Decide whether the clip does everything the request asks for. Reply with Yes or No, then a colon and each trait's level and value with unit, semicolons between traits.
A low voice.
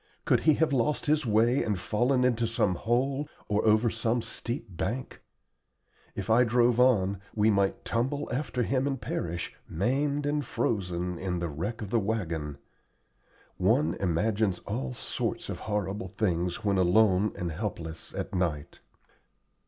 Yes: low, 110 Hz